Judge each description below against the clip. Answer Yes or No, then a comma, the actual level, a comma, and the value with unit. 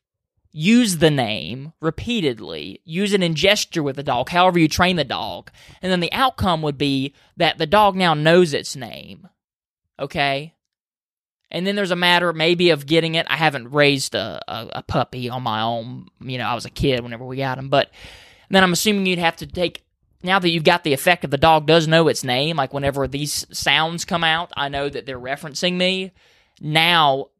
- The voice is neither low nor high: Yes, medium, 160 Hz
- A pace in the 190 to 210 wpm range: Yes, fast, 205 wpm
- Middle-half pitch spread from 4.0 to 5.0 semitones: Yes, average, 4.3 semitones